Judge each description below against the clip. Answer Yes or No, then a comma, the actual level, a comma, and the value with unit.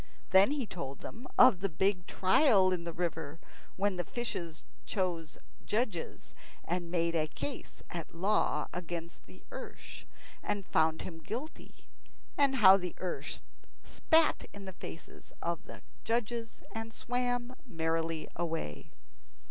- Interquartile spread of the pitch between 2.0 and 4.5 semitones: No, average, 5.3 semitones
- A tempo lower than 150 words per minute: Yes, slow, 135 wpm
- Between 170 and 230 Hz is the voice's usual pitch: Yes, medium, 185 Hz